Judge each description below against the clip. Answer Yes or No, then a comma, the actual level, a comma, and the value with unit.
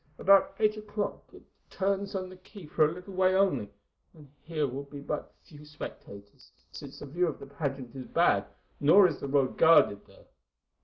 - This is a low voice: No, medium, 155 Hz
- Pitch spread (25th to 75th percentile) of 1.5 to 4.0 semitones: No, average, 5.3 semitones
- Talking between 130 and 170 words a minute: No, average, 195 wpm